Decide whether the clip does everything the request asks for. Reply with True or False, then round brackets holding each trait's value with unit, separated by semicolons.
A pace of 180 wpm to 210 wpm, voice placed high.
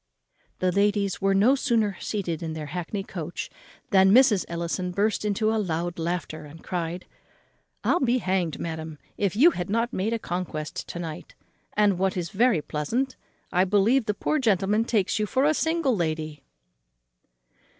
False (165 wpm; 195 Hz)